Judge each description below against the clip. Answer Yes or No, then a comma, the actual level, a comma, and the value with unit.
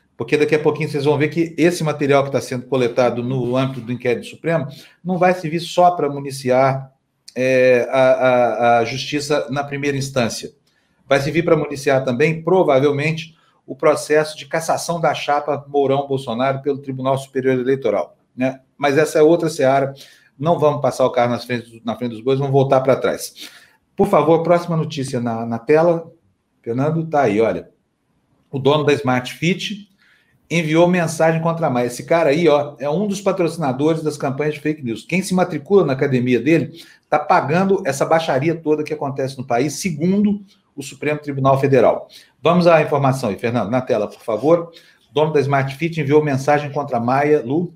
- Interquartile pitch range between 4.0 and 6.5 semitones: No, average, 3.5 semitones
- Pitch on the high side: No, medium, 145 Hz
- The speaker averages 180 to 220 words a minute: Yes, fast, 185 wpm